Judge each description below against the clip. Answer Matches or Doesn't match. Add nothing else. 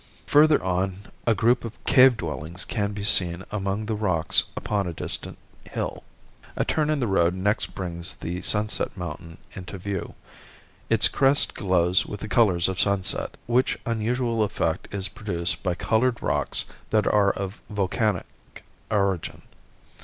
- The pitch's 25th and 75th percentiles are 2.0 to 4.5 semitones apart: Matches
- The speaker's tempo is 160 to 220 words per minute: Doesn't match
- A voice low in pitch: Matches